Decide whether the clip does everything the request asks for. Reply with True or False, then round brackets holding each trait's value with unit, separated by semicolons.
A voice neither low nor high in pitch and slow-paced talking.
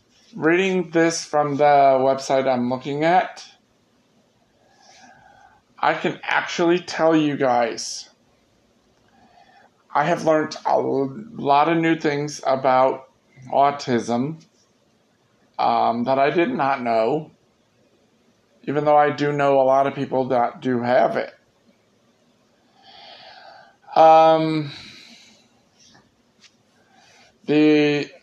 True (145 Hz; 95 wpm)